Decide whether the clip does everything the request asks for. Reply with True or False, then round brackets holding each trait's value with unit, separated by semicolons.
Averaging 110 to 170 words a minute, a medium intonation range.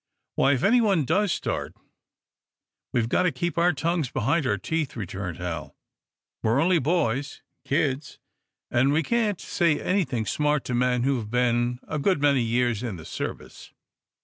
False (160 wpm; 5.7 semitones)